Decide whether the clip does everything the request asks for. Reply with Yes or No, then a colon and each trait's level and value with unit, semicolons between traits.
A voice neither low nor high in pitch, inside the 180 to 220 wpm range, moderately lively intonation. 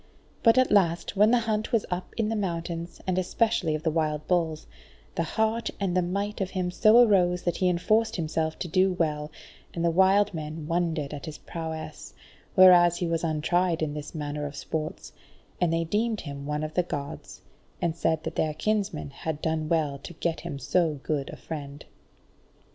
Yes: medium, 170 Hz; average, 195 wpm; average, 3.5 semitones